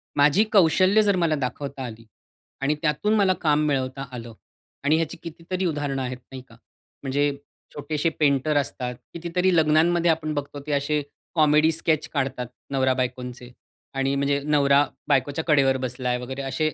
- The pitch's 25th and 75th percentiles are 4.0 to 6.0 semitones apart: No, average, 3.2 semitones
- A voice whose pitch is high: No, medium, 145 Hz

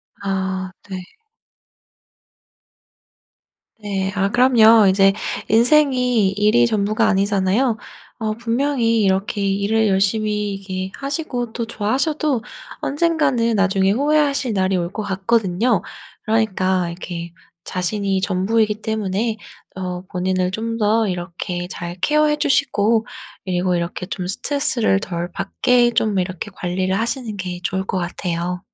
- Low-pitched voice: No, high, 205 Hz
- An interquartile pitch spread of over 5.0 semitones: No, average, 3.5 semitones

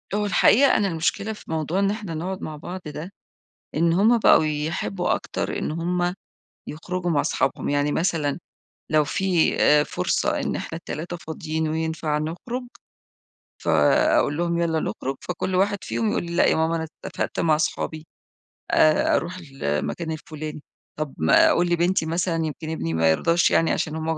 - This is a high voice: No, medium, 160 Hz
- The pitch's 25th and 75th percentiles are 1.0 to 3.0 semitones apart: Yes, narrow, 2.6 semitones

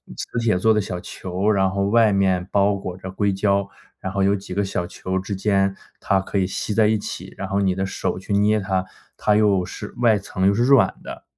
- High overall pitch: No, low, 100 Hz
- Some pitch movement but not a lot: No, narrow, 1.8 semitones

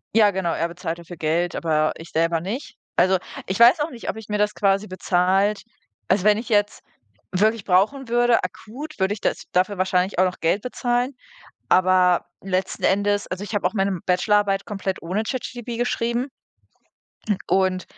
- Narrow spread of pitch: No, average, 3.4 semitones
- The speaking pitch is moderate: No, high, 195 Hz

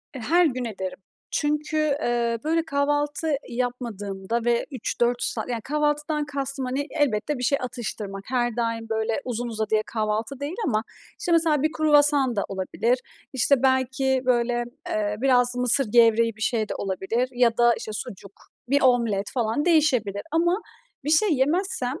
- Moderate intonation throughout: Yes, average, 4.3 semitones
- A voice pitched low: No, very high, 250 Hz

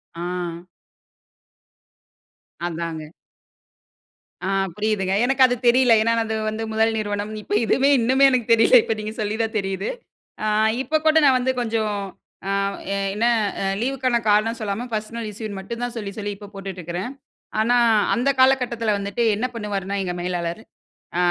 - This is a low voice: No, high, 215 Hz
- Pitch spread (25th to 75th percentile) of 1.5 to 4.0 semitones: Yes, average, 3.3 semitones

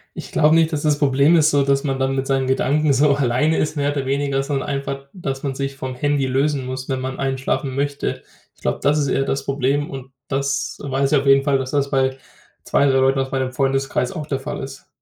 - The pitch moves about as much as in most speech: No, narrow, 1.3 semitones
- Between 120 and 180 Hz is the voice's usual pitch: Yes, low, 135 Hz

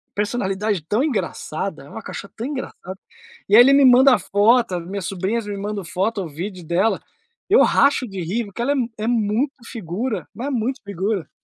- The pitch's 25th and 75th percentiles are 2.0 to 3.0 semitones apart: No, average, 4.1 semitones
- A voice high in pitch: Yes, high, 210 Hz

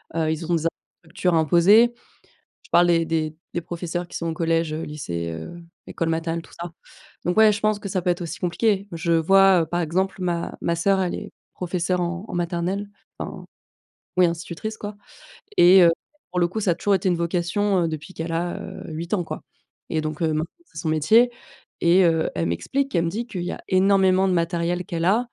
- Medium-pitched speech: Yes, medium, 175 Hz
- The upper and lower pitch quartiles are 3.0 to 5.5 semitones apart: No, narrow, 2.4 semitones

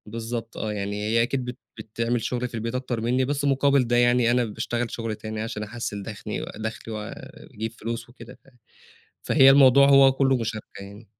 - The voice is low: Yes, low, 115 Hz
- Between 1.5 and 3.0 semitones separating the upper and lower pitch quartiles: Yes, narrow, 2.4 semitones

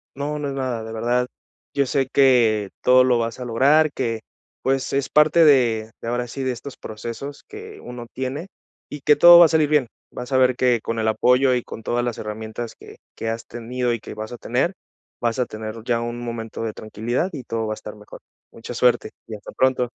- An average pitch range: Yes, average, 3.0 semitones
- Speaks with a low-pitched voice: Yes, low, 125 Hz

